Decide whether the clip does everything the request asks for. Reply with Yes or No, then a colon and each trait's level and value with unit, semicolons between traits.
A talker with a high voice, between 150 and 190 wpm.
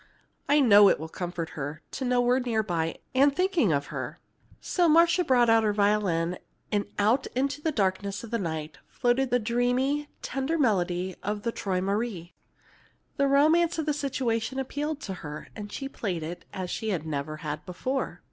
Yes: high, 220 Hz; average, 175 wpm